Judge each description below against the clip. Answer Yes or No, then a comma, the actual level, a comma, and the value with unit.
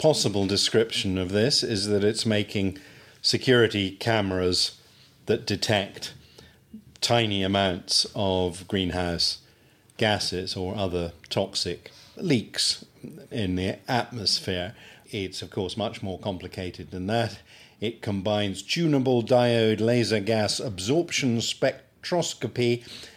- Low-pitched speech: Yes, low, 105 Hz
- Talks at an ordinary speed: No, slow, 105 wpm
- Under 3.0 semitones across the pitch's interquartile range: No, average, 4.1 semitones